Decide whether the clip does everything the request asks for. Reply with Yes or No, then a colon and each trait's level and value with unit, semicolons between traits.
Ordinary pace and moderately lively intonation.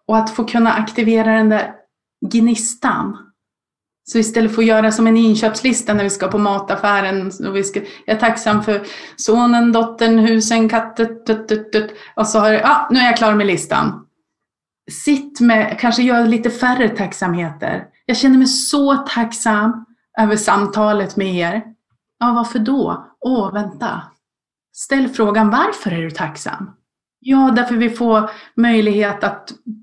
No: average, 155 wpm; narrow, 2.0 semitones